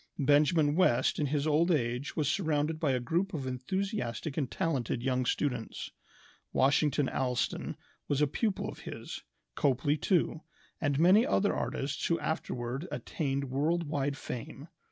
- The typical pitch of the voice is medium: Yes, medium, 145 Hz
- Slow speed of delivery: No, average, 145 wpm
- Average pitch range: Yes, average, 3.6 semitones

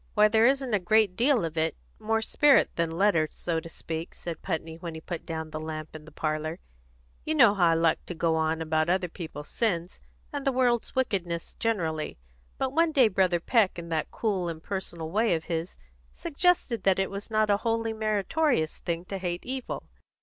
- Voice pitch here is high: No, medium, 180 Hz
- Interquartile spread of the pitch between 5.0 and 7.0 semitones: Yes, wide, 5.5 semitones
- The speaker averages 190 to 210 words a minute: Yes, average, 200 wpm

